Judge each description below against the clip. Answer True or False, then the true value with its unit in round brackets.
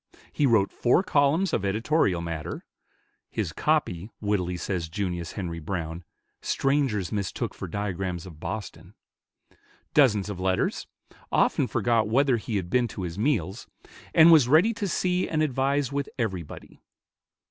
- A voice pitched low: True (105 Hz)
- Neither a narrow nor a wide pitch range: False (7.4 semitones)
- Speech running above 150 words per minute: False (140 wpm)